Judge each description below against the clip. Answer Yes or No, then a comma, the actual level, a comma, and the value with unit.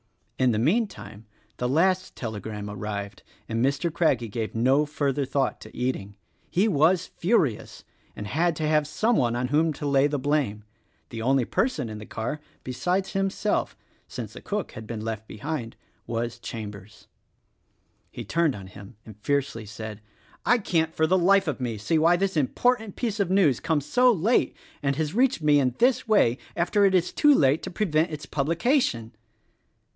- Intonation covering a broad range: Yes, wide, 7.7 semitones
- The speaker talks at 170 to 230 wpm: Yes, average, 180 wpm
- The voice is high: No, medium, 145 Hz